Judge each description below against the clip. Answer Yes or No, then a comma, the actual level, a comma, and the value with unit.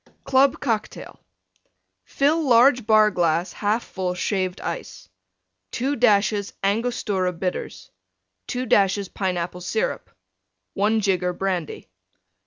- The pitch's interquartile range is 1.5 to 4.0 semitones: No, average, 4.6 semitones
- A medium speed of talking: No, slow, 100 wpm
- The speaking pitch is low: No, high, 205 Hz